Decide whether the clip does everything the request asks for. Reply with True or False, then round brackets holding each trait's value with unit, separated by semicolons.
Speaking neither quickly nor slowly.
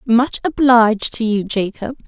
True (145 wpm)